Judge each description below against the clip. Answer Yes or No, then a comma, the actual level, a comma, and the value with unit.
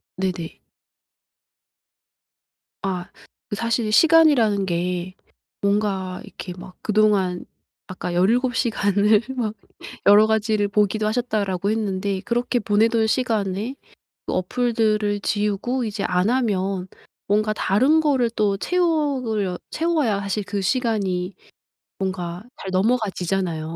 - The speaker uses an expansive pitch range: No, average, 3.4 semitones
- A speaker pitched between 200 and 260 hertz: Yes, high, 210 Hz